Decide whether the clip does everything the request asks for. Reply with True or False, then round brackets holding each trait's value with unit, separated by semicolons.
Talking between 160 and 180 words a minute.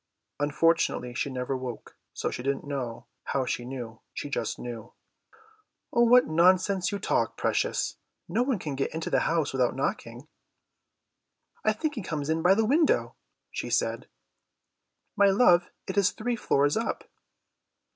False (150 wpm)